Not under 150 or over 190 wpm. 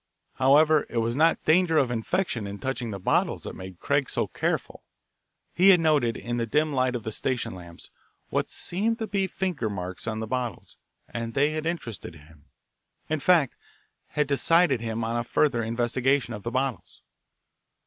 Yes: average, 180 wpm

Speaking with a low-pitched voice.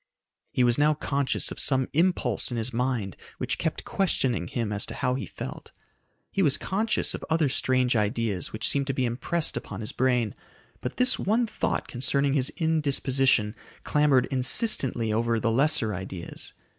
Yes: low, 130 Hz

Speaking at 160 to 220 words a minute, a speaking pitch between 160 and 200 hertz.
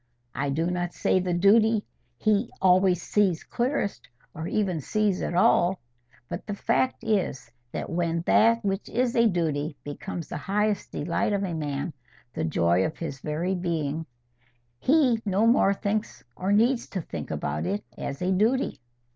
Yes: average, 165 wpm; medium, 185 Hz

